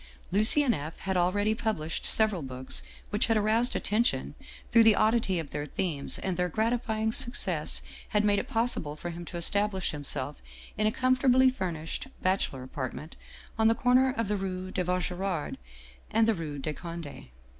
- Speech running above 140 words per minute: Yes, average, 175 wpm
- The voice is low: No, high, 195 Hz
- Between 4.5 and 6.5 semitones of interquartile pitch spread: Yes, average, 5.3 semitones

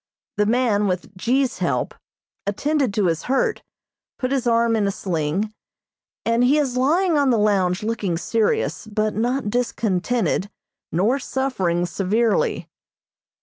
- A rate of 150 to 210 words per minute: No, slow, 135 wpm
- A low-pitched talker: No, high, 225 Hz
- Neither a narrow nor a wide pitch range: Yes, average, 4.4 semitones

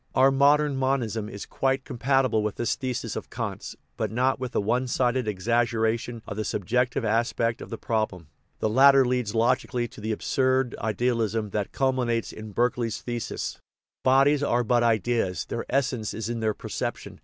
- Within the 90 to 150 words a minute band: No, average, 175 wpm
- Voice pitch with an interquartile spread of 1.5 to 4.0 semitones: Yes, average, 2.9 semitones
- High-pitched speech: No, low, 120 Hz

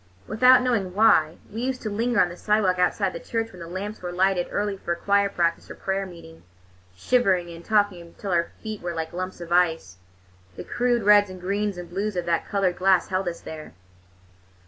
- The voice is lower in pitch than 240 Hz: Yes, medium, 185 Hz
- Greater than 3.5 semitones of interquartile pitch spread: No, average, 3.1 semitones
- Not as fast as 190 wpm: No, fast, 205 wpm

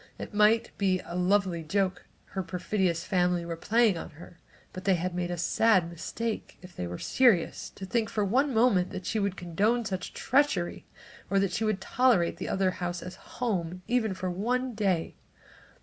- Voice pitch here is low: No, high, 190 Hz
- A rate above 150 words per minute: Yes, average, 180 wpm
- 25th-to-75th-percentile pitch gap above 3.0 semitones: Yes, average, 3.8 semitones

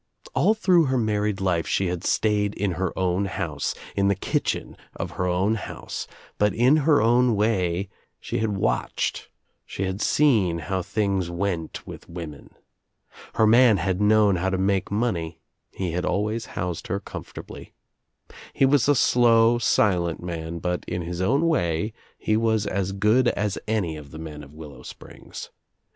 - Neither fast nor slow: Yes, average, 165 wpm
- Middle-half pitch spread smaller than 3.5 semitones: No, average, 4.0 semitones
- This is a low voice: Yes, low, 100 Hz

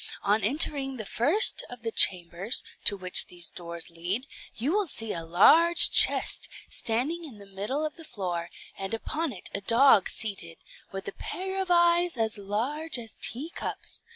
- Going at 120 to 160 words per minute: No, average, 170 wpm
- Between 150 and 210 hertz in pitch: No, high, 225 Hz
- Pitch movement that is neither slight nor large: No, wide, 8.0 semitones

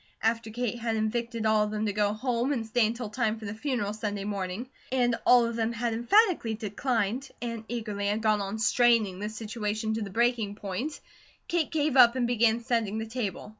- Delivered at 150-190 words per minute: No, fast, 205 wpm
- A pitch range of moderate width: No, narrow, 2.3 semitones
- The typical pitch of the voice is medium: No, high, 225 Hz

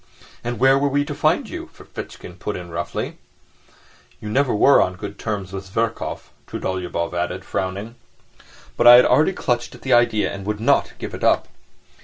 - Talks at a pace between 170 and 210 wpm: Yes, average, 180 wpm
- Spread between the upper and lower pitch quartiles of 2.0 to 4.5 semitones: No, average, 5.0 semitones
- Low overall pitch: Yes, low, 110 Hz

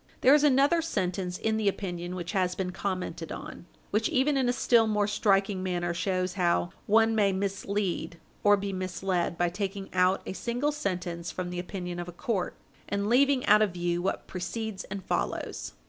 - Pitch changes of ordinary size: Yes, average, 3.4 semitones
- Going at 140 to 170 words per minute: No, average, 185 wpm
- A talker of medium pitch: No, high, 195 Hz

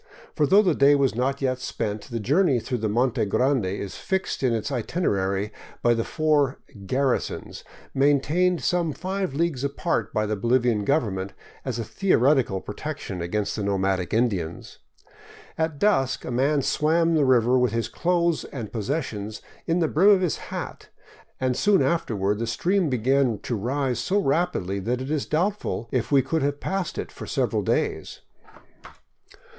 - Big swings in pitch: Yes, wide, 5.9 semitones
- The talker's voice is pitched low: Yes, low, 130 Hz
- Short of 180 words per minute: Yes, average, 170 wpm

